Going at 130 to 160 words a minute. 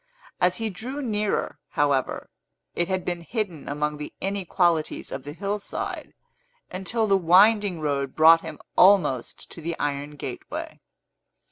Yes: slow, 135 wpm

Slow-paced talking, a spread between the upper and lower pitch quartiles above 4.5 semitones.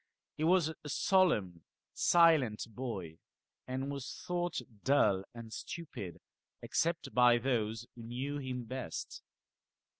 Yes: slow, 115 wpm; wide, 5.6 semitones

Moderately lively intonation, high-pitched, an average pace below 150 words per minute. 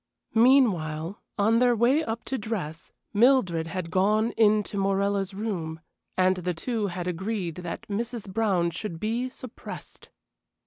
Yes: average, 4.1 semitones; high, 200 Hz; average, 140 wpm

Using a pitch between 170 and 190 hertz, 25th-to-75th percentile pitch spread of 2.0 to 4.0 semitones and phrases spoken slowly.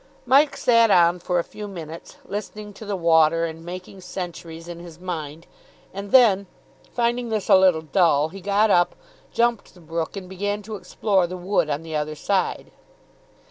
No: medium, 185 Hz; average, 3.7 semitones; average, 180 wpm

